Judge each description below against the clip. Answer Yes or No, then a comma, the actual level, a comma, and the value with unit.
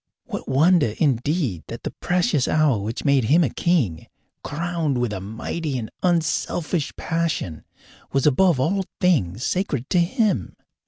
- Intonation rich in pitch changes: Yes, wide, 6.1 semitones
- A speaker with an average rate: Yes, average, 145 wpm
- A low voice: No, medium, 150 Hz